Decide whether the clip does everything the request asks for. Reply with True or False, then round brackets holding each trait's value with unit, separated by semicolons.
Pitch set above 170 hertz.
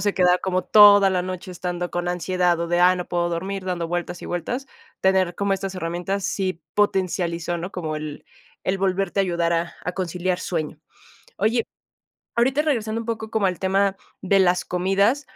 True (185 Hz)